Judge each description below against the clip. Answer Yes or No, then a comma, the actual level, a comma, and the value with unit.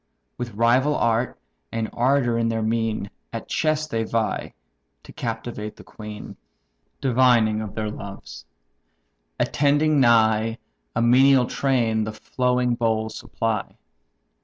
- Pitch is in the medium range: No, low, 115 Hz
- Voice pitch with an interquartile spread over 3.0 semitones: No, narrow, 2.5 semitones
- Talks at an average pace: No, slow, 120 wpm